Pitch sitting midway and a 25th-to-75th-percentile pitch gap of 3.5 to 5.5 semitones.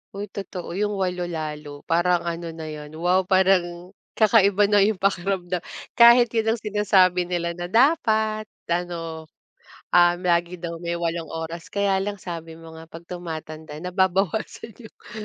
No: medium, 180 Hz; average, 3.0 semitones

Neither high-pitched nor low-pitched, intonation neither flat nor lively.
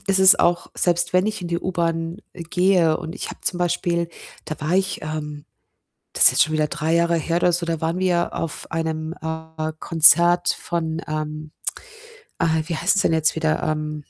No: medium, 165 Hz; narrow, 1.8 semitones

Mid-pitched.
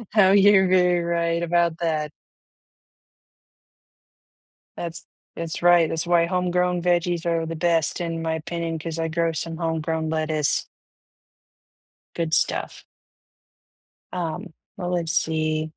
Yes: medium, 170 Hz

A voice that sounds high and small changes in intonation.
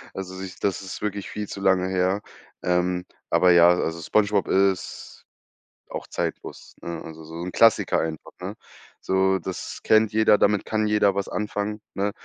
No: very low, 95 Hz; narrow, 2.3 semitones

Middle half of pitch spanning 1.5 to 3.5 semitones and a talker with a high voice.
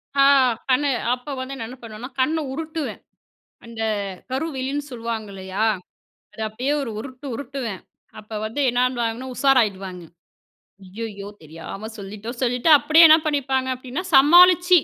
No: average, 4.2 semitones; very high, 250 Hz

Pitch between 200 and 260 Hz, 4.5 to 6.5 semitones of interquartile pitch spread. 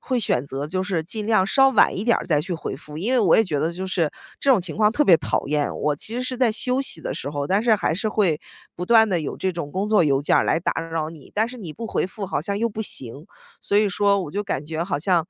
No: medium, 185 Hz; wide, 5.5 semitones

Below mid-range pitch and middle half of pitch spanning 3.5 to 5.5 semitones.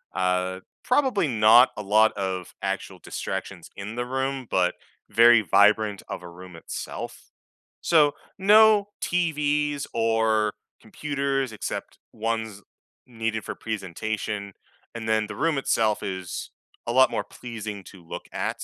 Yes: low, 110 Hz; average, 4.9 semitones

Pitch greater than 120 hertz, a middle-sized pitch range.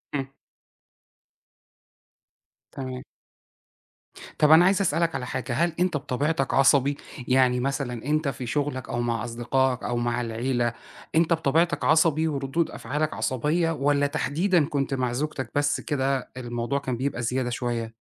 Yes: low, 135 Hz; average, 3.5 semitones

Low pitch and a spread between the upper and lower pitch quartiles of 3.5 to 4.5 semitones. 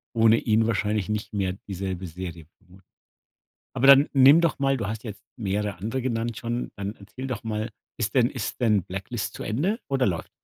Yes: low, 110 Hz; average, 3.9 semitones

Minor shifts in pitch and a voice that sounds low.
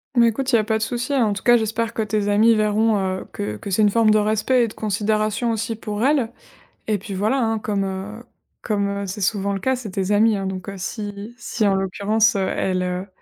No: narrow, 2.2 semitones; high, 215 Hz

